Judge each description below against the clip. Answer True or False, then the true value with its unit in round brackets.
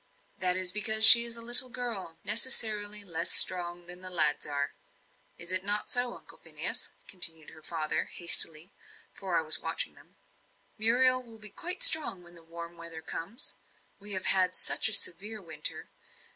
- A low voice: False (185 Hz)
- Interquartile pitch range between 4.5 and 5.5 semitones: True (4.8 semitones)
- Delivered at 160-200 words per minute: True (170 wpm)